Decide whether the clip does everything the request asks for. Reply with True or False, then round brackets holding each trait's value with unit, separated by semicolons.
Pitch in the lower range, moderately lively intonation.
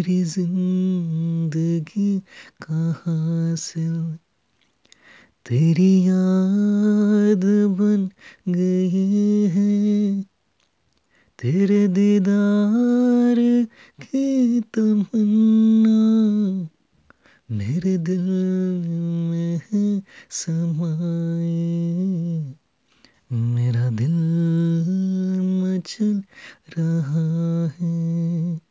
False (185 Hz; 3.7 semitones)